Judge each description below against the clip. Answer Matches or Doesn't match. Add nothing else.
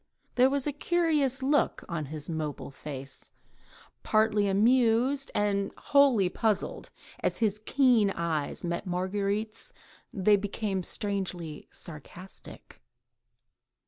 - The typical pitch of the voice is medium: Doesn't match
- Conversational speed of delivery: Doesn't match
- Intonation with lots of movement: Matches